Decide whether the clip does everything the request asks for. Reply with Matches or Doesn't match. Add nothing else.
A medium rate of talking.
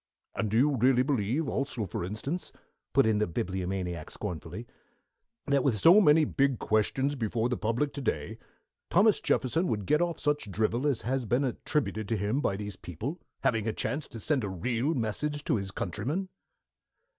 Matches